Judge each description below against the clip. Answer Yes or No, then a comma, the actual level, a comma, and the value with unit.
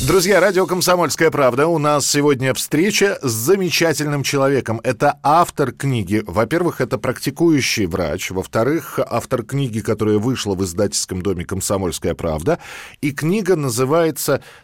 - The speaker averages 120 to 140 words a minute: Yes, average, 125 wpm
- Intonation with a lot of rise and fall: Yes, wide, 6.5 semitones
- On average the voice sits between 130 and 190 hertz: Yes, low, 135 Hz